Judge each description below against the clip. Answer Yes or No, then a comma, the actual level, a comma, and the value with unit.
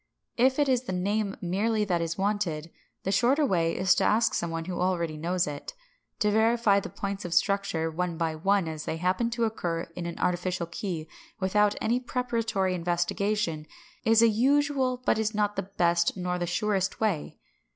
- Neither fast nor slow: Yes, average, 185 wpm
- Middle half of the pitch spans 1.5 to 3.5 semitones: No, average, 4.3 semitones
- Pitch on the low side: No, high, 195 Hz